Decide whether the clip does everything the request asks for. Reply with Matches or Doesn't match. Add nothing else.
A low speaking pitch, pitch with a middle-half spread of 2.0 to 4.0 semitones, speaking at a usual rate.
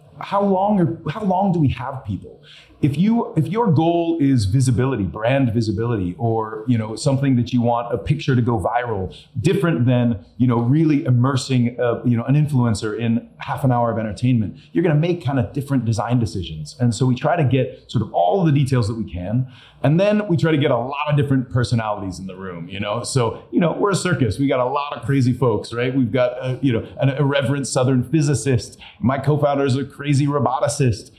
Doesn't match